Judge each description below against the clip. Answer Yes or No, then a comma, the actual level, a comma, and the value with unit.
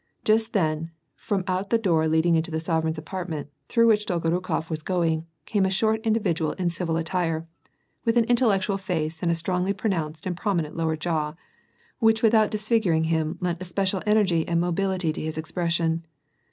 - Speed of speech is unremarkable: Yes, average, 180 wpm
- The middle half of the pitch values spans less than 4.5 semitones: Yes, average, 3.6 semitones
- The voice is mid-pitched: Yes, medium, 175 Hz